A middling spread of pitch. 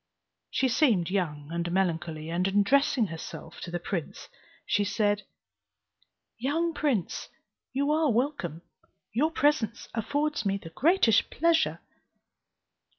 No: wide, 8.7 semitones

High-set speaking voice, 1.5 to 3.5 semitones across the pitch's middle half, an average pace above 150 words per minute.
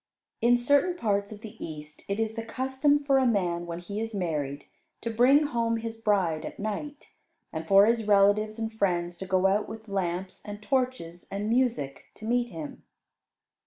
No: high, 215 Hz; average, 4.3 semitones; average, 185 wpm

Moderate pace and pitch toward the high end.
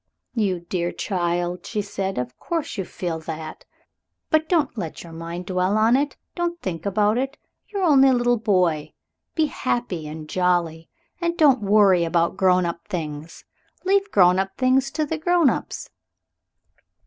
Yes: average, 160 wpm; high, 195 Hz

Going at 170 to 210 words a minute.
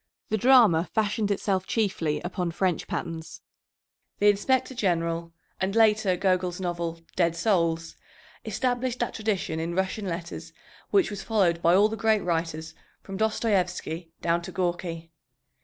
No: average, 140 wpm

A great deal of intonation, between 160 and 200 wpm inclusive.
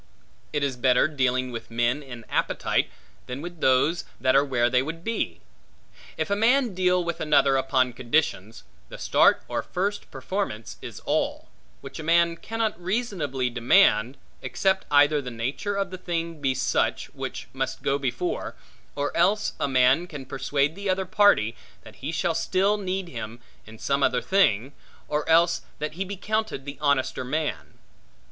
Yes: wide, 6.1 semitones; average, 165 wpm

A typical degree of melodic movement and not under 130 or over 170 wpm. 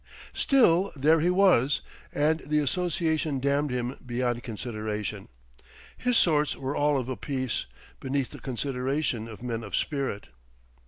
Yes: average, 4.1 semitones; average, 140 wpm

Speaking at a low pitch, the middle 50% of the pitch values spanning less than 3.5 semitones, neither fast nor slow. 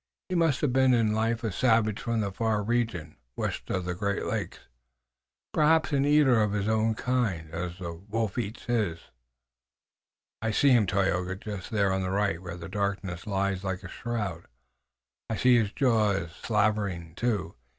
No: low, 105 Hz; average, 3.8 semitones; average, 170 wpm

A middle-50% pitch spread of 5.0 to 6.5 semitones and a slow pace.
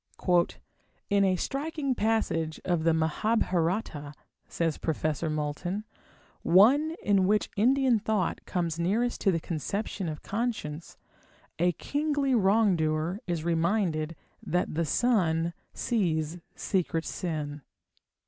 Yes: wide, 5.4 semitones; slow, 110 wpm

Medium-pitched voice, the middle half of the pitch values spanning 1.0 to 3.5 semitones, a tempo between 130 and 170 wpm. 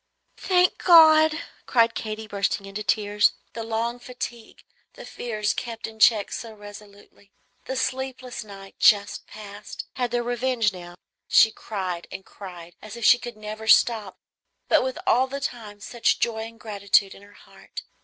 No: high, 220 Hz; average, 2.9 semitones; average, 165 wpm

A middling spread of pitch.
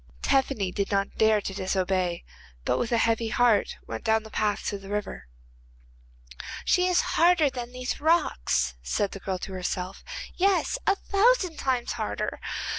No: wide, 5.9 semitones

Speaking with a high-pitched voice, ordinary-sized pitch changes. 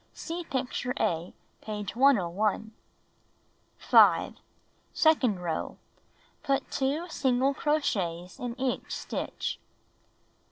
No: very high, 250 Hz; wide, 6.0 semitones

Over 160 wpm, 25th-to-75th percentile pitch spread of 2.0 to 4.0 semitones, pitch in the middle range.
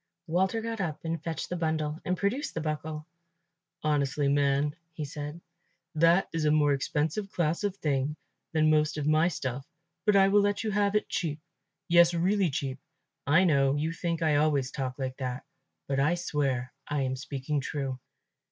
Yes: average, 180 wpm; average, 3.4 semitones; medium, 155 Hz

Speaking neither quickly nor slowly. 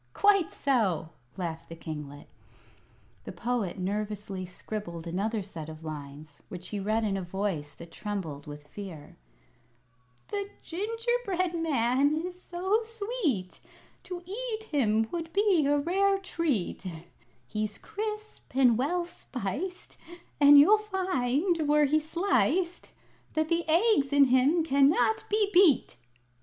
No: slow, 125 wpm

